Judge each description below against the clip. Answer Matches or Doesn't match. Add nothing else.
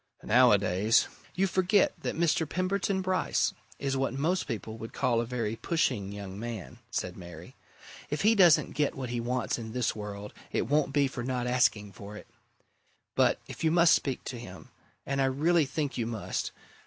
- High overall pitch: Doesn't match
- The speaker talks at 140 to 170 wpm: Doesn't match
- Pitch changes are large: Matches